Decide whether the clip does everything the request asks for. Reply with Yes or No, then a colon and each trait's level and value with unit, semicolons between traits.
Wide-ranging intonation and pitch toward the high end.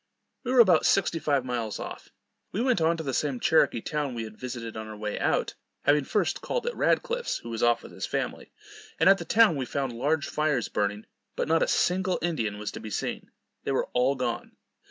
No: wide, 6.6 semitones; medium, 140 Hz